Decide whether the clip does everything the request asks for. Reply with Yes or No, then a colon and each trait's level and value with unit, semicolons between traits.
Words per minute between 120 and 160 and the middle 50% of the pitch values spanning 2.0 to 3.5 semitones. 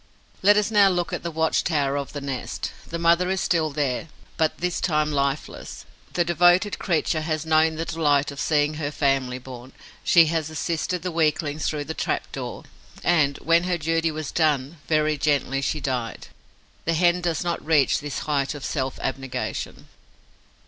No: average, 175 wpm; average, 3.0 semitones